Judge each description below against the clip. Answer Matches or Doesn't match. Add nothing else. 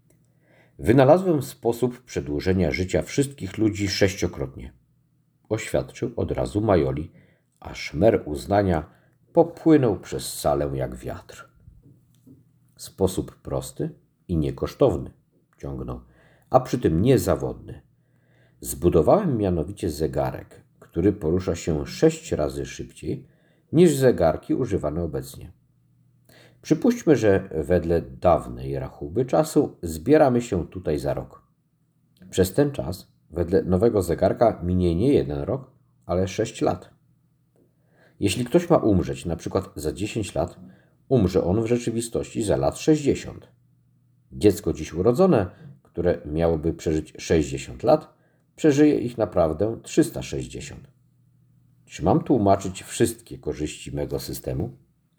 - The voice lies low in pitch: Matches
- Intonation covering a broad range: Matches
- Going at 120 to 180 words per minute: Doesn't match